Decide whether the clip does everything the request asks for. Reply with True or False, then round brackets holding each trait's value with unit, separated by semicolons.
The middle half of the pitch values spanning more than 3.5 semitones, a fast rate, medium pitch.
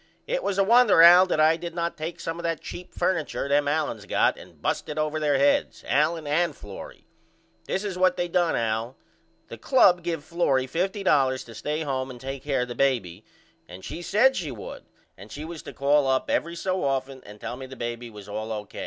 True (4.8 semitones; 220 wpm; 150 Hz)